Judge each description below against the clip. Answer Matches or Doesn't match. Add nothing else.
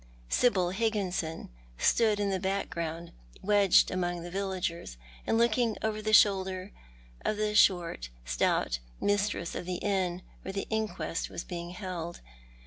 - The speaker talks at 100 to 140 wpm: Matches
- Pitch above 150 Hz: Matches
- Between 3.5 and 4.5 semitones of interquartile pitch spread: Doesn't match